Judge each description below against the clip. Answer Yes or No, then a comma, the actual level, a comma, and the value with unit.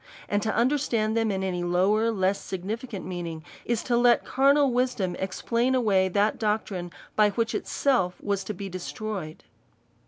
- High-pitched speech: Yes, high, 210 Hz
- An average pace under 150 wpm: No, average, 160 wpm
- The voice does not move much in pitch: No, average, 3.8 semitones